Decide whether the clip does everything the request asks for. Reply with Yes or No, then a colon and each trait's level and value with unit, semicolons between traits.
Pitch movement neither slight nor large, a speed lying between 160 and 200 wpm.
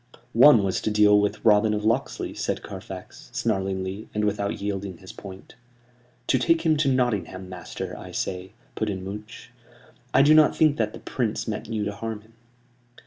Yes: average, 3.0 semitones; average, 180 wpm